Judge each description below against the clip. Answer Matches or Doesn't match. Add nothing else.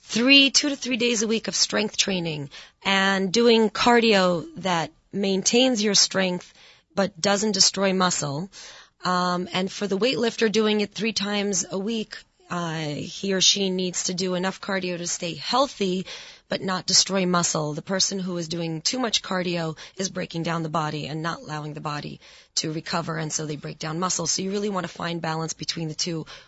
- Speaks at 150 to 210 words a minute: Matches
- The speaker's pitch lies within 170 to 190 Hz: Matches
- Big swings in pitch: Doesn't match